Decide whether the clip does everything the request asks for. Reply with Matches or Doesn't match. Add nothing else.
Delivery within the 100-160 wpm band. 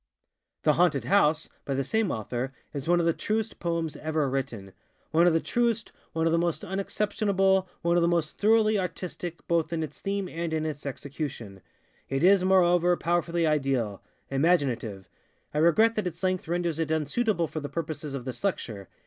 Doesn't match